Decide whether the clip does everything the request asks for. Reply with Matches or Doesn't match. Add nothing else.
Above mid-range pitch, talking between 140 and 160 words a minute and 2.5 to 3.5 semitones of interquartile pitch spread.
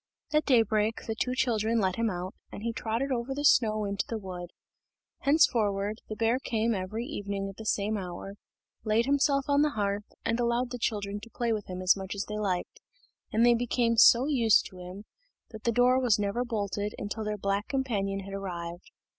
Doesn't match